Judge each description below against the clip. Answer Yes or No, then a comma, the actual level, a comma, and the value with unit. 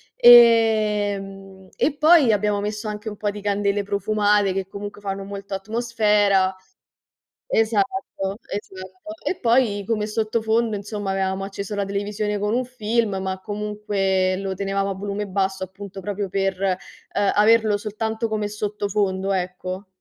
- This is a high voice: Yes, high, 205 Hz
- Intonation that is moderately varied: No, narrow, 1.7 semitones